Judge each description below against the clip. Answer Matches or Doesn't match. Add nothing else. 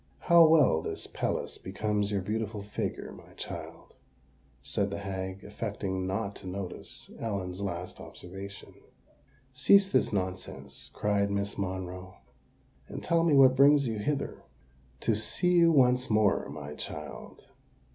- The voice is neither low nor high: Doesn't match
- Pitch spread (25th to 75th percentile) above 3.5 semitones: Matches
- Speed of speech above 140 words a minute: Doesn't match